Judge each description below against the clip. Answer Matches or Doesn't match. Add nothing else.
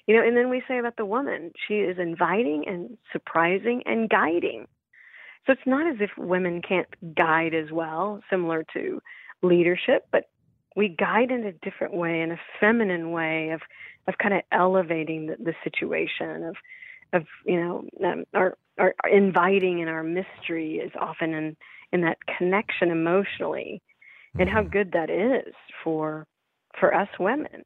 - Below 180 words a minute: Matches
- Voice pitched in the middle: Matches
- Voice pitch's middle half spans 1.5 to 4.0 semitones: Doesn't match